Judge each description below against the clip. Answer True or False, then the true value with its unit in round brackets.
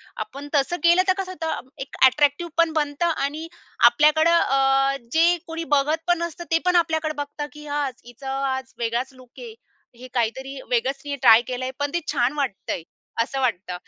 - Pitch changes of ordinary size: True (3.6 semitones)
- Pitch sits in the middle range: False (280 Hz)